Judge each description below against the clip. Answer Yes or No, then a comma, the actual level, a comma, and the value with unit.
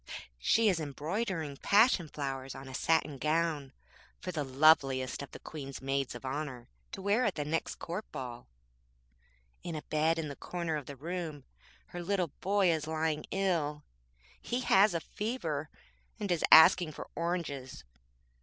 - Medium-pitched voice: Yes, medium, 155 Hz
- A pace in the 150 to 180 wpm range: Yes, average, 160 wpm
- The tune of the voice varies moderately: Yes, average, 4.1 semitones